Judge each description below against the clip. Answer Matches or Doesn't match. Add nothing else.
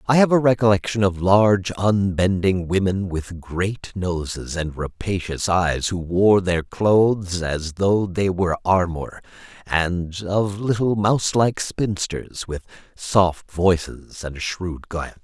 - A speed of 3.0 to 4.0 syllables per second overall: Matches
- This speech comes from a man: Matches